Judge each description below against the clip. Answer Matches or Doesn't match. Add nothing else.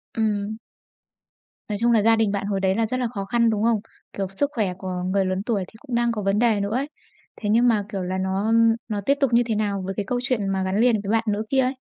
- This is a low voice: Doesn't match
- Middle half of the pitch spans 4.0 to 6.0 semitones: Doesn't match